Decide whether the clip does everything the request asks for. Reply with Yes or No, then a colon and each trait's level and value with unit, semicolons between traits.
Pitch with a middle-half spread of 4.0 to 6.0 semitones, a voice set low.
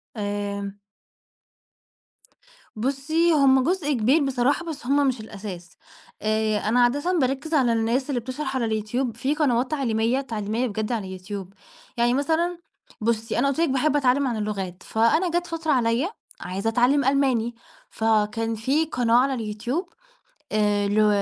No: average, 4.4 semitones; high, 245 Hz